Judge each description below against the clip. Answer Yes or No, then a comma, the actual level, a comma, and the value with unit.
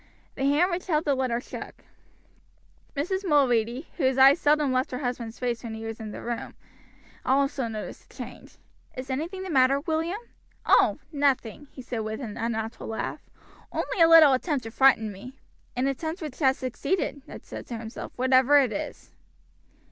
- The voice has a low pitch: No, very high, 265 Hz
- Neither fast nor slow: Yes, average, 175 wpm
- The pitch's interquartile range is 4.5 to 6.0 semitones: No, average, 3.8 semitones